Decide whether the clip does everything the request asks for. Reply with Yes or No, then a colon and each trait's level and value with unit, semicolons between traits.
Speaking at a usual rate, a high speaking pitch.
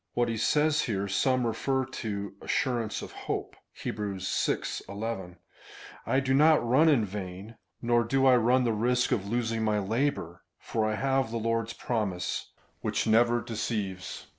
No: average, 165 wpm; low, 115 Hz